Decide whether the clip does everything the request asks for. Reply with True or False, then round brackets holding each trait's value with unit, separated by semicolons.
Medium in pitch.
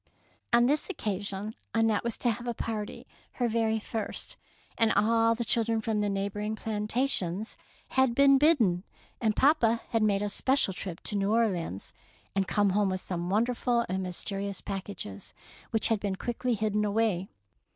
False (215 Hz)